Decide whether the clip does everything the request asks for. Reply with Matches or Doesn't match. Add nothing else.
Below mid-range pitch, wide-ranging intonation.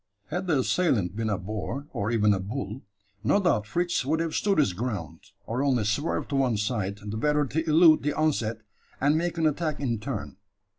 Matches